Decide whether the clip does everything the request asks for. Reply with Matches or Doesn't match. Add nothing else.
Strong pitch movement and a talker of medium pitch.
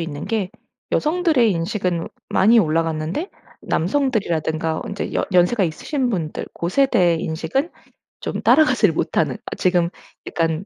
Matches